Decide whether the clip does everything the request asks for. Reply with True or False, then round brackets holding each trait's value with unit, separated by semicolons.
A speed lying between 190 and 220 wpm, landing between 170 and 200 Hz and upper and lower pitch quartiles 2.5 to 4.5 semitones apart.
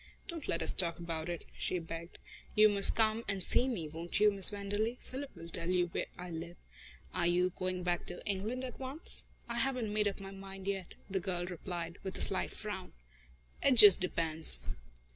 True (200 wpm; 190 Hz; 3.5 semitones)